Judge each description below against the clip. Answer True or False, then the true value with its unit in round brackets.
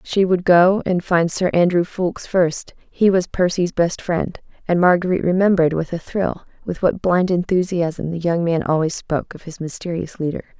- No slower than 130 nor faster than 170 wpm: False (185 wpm)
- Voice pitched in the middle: True (175 Hz)